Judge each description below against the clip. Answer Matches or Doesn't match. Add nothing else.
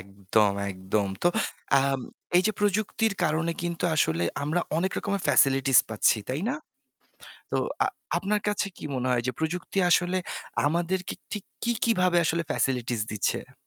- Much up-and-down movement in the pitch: Matches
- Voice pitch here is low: Doesn't match